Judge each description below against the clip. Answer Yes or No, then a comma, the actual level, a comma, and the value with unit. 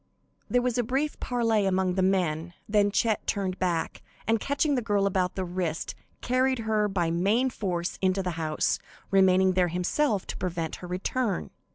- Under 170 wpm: No, average, 175 wpm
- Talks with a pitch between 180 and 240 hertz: Yes, high, 190 Hz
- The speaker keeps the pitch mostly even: No, average, 4.0 semitones